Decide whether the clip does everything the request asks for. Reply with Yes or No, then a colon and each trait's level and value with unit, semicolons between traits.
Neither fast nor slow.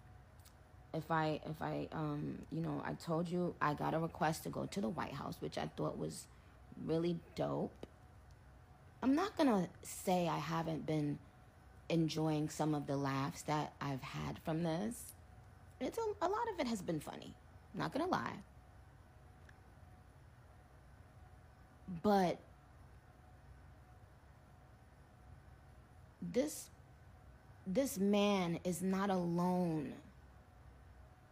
No: slow, 125 wpm